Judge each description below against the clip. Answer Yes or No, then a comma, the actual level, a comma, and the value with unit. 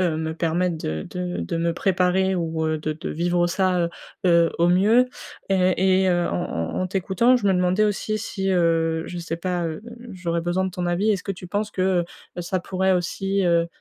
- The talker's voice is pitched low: No, medium, 180 Hz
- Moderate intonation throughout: No, narrow, 2.0 semitones